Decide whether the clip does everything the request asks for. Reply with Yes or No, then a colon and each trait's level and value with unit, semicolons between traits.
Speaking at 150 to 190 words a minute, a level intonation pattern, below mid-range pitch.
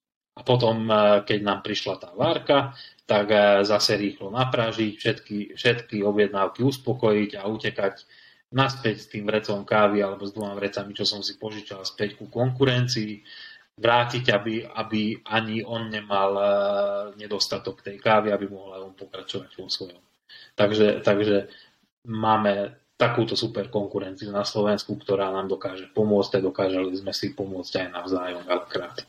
No: average, 140 wpm; narrow, 1.6 semitones; low, 105 Hz